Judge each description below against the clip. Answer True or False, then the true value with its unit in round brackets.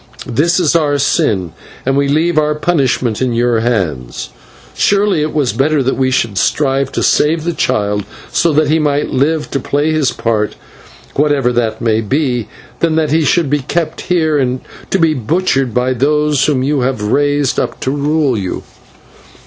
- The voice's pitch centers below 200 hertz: True (140 Hz)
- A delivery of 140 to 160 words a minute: False (175 wpm)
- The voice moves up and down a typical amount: True (4.0 semitones)